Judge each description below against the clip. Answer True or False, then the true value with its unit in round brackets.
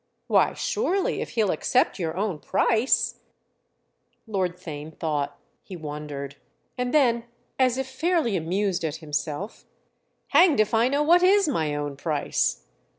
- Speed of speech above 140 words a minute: False (135 wpm)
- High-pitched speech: True (195 Hz)